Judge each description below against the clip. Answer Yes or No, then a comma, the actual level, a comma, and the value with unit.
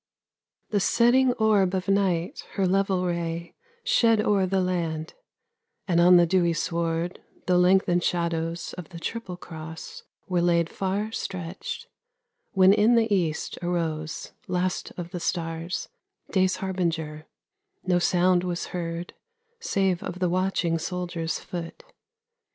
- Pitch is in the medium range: Yes, medium, 180 Hz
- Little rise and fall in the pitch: Yes, narrow, 2.2 semitones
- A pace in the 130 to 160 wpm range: Yes, slow, 135 wpm